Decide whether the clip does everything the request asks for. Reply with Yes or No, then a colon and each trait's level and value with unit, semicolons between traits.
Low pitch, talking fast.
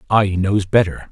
No: low, 100 Hz; average, 160 wpm